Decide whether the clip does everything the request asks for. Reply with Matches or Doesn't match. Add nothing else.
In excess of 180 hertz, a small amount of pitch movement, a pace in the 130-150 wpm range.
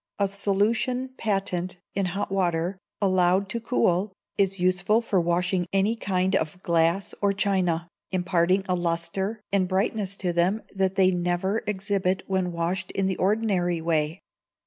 Matches